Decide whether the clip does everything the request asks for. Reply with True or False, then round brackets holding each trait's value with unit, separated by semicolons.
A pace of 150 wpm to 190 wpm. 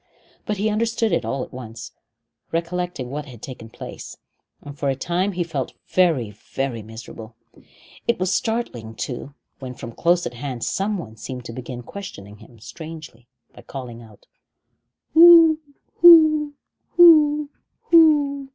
False (140 wpm)